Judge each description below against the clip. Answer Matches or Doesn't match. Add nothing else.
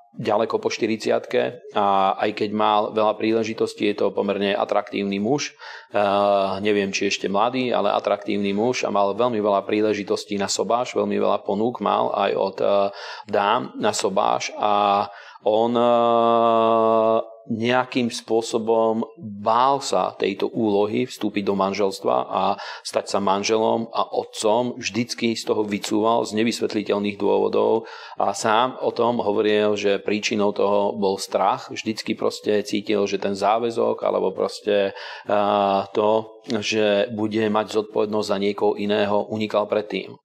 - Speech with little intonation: Matches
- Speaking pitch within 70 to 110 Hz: Matches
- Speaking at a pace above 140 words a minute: Doesn't match